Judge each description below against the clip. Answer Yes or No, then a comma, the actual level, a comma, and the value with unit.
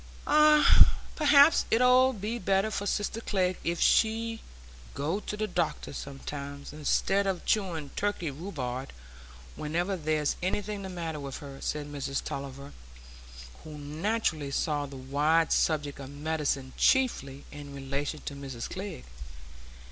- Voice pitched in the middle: Yes, medium, 155 Hz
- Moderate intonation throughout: No, wide, 6.2 semitones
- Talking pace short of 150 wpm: Yes, slow, 135 wpm